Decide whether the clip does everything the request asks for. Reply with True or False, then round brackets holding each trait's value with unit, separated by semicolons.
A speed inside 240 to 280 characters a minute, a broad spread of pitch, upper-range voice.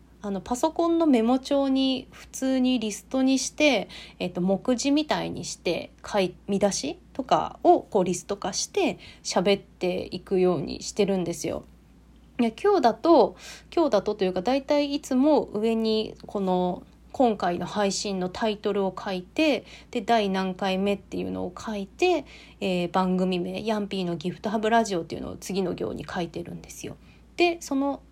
False (320 characters per minute; 6.0 semitones; 210 Hz)